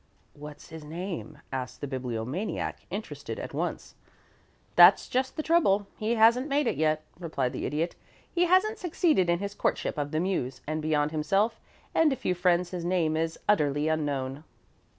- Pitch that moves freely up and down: Yes, wide, 6.3 semitones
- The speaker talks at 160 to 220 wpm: Yes, average, 170 wpm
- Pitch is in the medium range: Yes, medium, 170 Hz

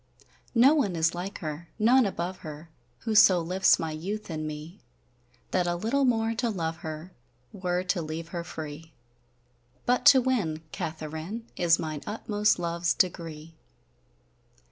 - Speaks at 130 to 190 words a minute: Yes, average, 145 wpm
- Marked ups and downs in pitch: No, average, 4.6 semitones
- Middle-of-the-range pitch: Yes, medium, 175 Hz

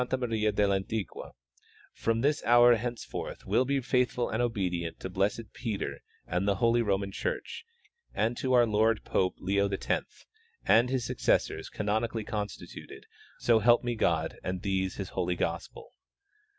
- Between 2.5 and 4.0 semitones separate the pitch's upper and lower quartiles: Yes, average, 3.5 semitones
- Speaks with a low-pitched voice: Yes, low, 110 Hz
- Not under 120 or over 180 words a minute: Yes, average, 150 wpm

